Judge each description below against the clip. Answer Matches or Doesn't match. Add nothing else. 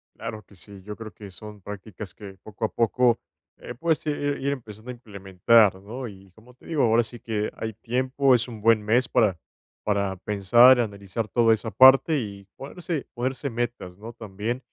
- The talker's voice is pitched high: Doesn't match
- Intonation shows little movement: Doesn't match